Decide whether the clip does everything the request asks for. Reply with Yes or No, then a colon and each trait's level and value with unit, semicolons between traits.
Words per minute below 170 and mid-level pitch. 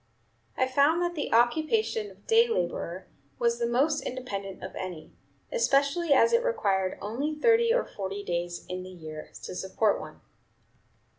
No: average, 155 wpm; very high, 250 Hz